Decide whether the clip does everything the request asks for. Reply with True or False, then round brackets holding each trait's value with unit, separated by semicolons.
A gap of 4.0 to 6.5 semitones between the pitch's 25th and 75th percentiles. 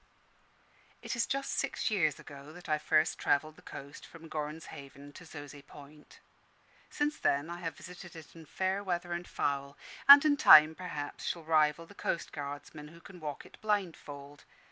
False (3.5 semitones)